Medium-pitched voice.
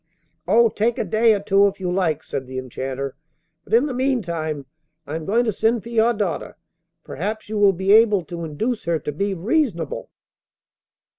No: high, 200 Hz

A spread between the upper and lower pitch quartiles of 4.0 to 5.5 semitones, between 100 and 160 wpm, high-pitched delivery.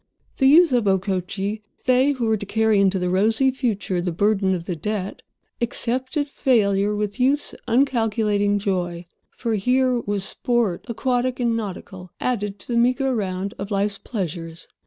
Yes: average, 4.3 semitones; average, 150 wpm; high, 210 Hz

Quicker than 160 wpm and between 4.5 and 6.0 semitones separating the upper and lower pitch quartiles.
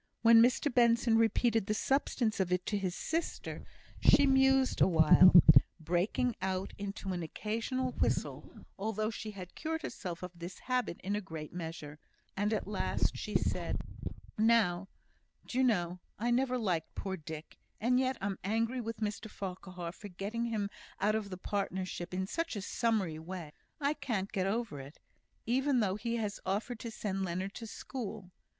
No: average, 170 wpm; average, 4.1 semitones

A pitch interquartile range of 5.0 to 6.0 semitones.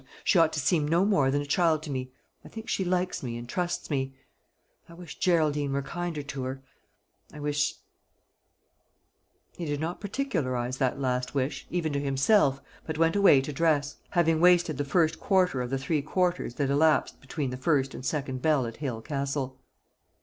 No: average, 3.9 semitones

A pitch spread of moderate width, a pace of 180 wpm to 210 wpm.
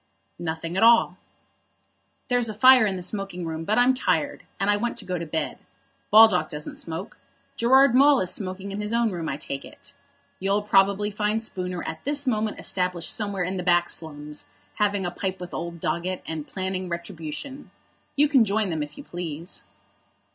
Yes: average, 4.2 semitones; average, 185 wpm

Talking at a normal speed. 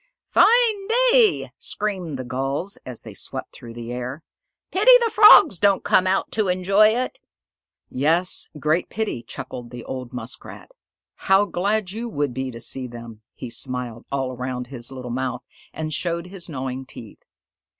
Yes: average, 160 wpm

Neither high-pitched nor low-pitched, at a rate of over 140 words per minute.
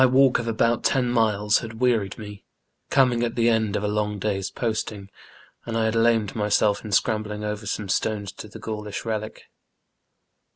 No: low, 110 Hz; average, 175 wpm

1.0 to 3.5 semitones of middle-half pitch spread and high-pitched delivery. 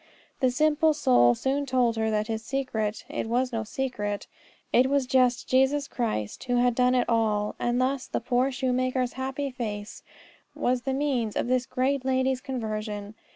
Yes: average, 2.9 semitones; very high, 250 Hz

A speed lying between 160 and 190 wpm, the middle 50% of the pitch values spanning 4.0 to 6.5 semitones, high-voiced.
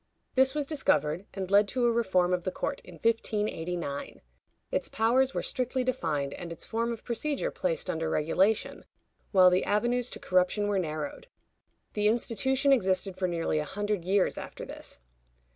Yes: average, 165 wpm; average, 5.2 semitones; high, 205 Hz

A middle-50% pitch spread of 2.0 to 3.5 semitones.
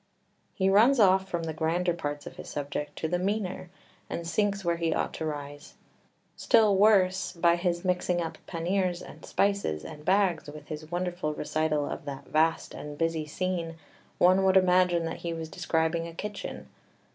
Yes: average, 2.8 semitones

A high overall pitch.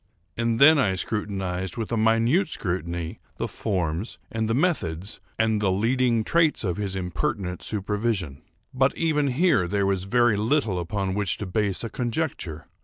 No: low, 105 Hz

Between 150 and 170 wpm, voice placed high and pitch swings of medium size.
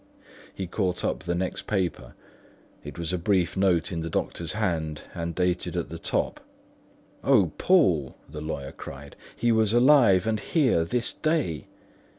No: average, 160 wpm; very low, 90 Hz; average, 5.0 semitones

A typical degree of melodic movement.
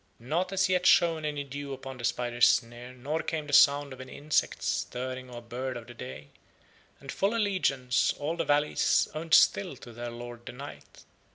Yes: average, 4.0 semitones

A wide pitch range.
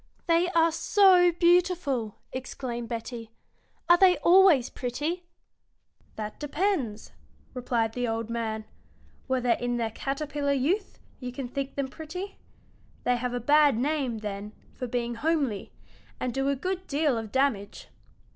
Yes: wide, 5.7 semitones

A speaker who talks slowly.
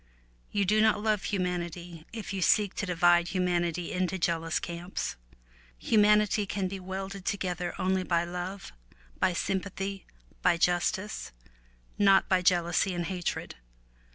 Yes: slow, 130 wpm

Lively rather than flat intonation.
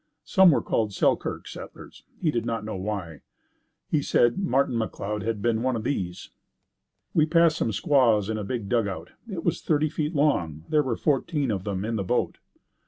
Yes: wide, 6.4 semitones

